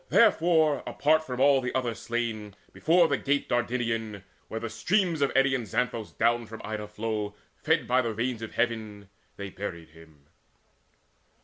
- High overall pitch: No, low, 115 Hz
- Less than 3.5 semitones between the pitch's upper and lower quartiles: No, average, 4.0 semitones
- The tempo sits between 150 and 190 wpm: Yes, average, 155 wpm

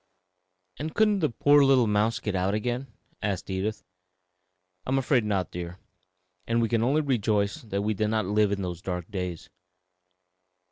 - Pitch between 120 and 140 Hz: No, low, 105 Hz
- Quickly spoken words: No, average, 170 wpm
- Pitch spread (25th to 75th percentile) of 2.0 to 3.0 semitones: No, average, 4.3 semitones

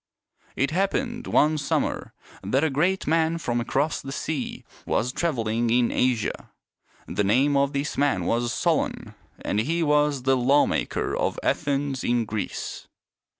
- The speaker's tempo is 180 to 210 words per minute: No, average, 145 wpm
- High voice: No, medium, 140 Hz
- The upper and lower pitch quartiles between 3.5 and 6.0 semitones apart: Yes, average, 4.0 semitones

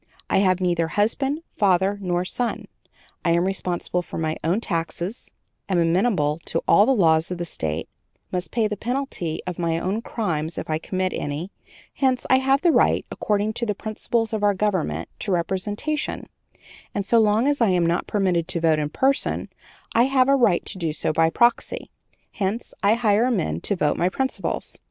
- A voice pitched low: No, high, 190 Hz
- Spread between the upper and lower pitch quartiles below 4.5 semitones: No, average, 5.1 semitones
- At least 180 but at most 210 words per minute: Yes, average, 190 wpm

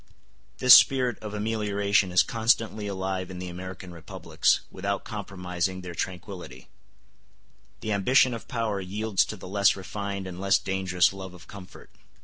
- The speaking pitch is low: Yes, very low, 95 Hz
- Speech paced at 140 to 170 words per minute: Yes, average, 145 wpm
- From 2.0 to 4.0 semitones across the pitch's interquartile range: Yes, narrow, 2.4 semitones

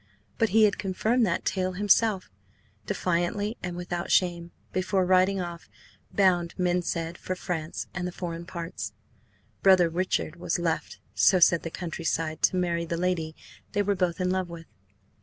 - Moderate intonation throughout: No, narrow, 1.7 semitones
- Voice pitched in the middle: Yes, medium, 180 Hz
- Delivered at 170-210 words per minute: No, average, 160 wpm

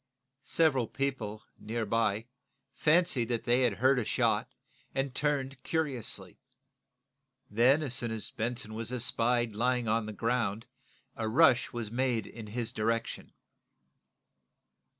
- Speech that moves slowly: Yes, slow, 125 wpm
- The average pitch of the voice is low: Yes, low, 120 Hz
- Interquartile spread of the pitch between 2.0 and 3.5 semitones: Yes, average, 2.8 semitones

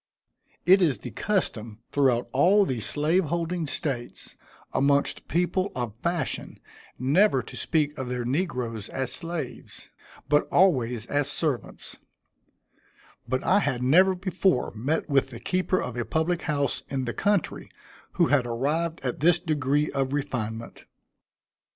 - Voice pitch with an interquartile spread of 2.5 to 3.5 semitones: No, wide, 5.4 semitones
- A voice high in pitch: No, medium, 145 Hz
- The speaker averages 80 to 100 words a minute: No, average, 140 wpm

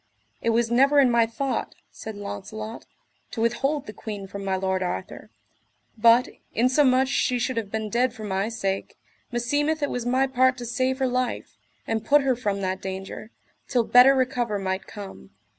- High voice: Yes, high, 235 Hz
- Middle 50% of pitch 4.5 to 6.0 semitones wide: No, average, 3.9 semitones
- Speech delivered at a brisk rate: No, average, 175 wpm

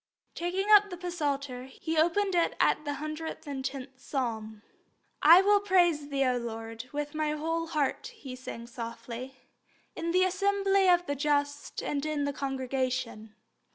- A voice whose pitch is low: No, very high, 290 Hz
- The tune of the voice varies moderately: Yes, average, 5.0 semitones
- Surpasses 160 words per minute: No, average, 150 wpm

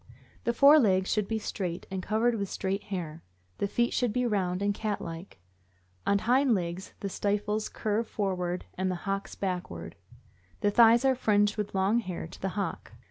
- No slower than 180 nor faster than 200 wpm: Yes, average, 185 wpm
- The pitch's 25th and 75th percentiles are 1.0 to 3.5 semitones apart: Yes, average, 2.8 semitones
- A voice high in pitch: Yes, high, 200 Hz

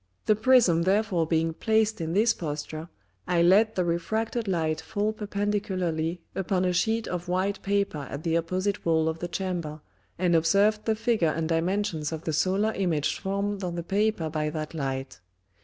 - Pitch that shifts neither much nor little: Yes, average, 4.1 semitones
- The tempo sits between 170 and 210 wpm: Yes, average, 175 wpm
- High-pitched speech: No, medium, 180 Hz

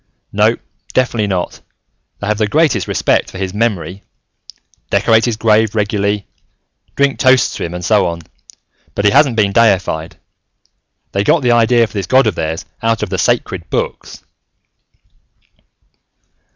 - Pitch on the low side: Yes, low, 105 Hz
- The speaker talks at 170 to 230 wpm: No, average, 150 wpm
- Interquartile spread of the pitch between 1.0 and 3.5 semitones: Yes, average, 3.1 semitones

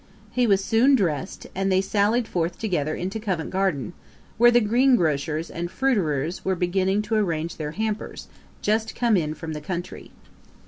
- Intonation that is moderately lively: Yes, average, 4.8 semitones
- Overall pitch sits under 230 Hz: Yes, high, 190 Hz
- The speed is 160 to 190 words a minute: Yes, average, 165 wpm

